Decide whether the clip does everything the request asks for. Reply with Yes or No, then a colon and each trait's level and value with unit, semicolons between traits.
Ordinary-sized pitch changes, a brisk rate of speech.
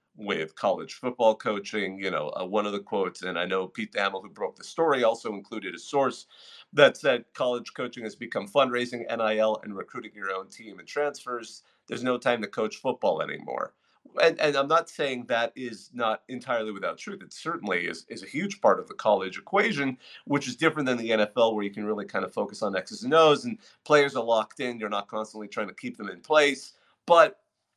Yes: average, 4.1 semitones; fast, 215 wpm